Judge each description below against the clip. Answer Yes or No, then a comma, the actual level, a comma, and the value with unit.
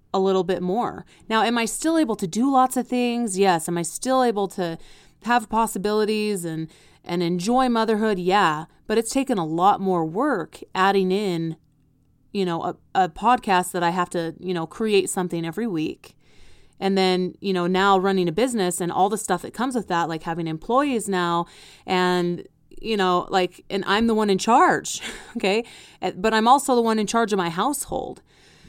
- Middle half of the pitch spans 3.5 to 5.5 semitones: Yes, average, 4.1 semitones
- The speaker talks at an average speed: Yes, average, 190 wpm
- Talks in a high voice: Yes, high, 195 Hz